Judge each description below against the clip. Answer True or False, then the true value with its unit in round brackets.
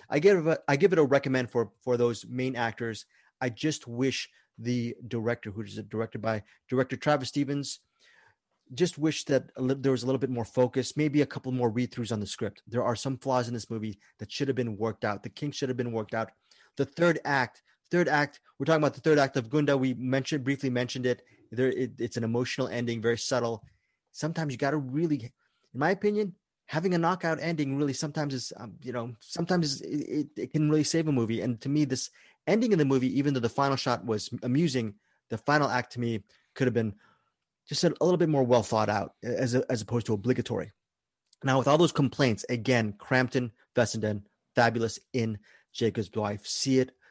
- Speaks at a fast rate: True (215 wpm)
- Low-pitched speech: True (130 Hz)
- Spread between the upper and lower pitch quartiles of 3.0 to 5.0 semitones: True (3.7 semitones)